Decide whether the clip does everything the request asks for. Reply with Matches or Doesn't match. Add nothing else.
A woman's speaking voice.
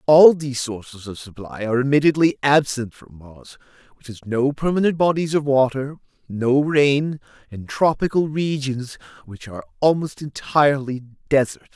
Doesn't match